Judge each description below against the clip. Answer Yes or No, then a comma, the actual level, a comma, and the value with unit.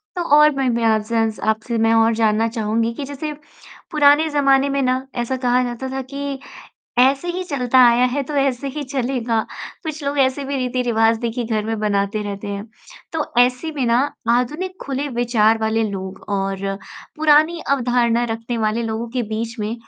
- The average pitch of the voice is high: Yes, high, 245 Hz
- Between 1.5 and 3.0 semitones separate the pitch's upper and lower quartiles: No, average, 3.6 semitones